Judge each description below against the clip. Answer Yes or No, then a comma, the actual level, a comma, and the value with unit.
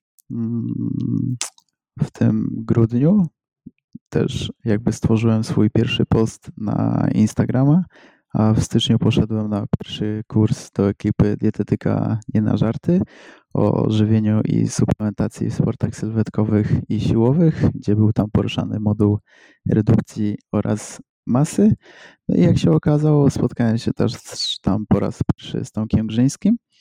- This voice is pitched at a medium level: No, low, 110 Hz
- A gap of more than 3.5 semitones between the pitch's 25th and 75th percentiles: No, average, 3.2 semitones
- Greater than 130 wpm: No, average, 125 wpm